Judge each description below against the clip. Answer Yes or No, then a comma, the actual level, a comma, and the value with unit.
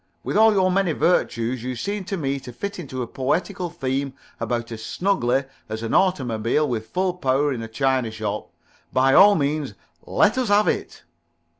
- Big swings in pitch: Yes, wide, 7.4 semitones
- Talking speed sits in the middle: Yes, average, 185 wpm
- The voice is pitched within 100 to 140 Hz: Yes, low, 135 Hz